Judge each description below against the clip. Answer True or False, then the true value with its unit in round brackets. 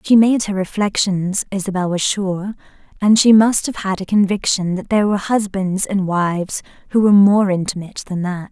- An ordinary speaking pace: True (185 wpm)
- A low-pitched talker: False (195 Hz)